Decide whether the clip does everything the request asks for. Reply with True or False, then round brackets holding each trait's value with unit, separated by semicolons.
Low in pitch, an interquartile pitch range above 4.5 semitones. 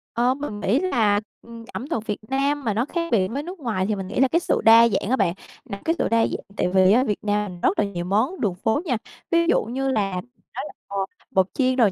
False (230 Hz; 4.9 semitones)